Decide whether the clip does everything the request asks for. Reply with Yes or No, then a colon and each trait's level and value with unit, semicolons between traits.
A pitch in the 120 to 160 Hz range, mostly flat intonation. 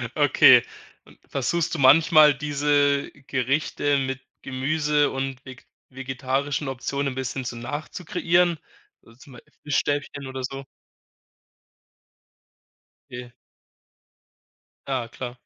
Yes: low, 135 Hz; narrow, 2.0 semitones